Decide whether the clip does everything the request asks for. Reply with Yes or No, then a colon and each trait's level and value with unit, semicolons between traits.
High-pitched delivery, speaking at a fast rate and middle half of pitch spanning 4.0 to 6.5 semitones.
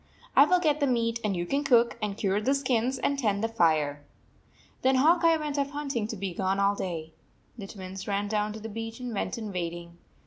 Yes: high, 220 Hz; fast, 230 wpm; wide, 5.5 semitones